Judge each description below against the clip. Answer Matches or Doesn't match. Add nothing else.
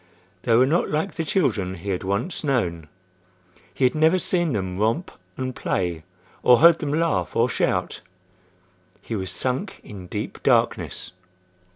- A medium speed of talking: Matches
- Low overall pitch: Matches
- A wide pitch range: Matches